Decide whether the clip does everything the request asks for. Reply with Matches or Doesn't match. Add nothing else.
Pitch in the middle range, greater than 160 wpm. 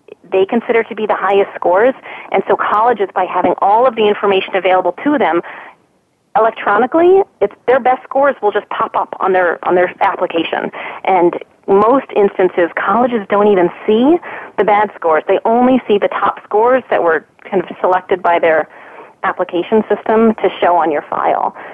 Doesn't match